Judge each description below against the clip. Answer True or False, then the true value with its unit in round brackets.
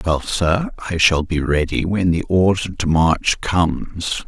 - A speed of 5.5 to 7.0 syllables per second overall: False (3.8 syllables/s)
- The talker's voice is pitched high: False (85 Hz)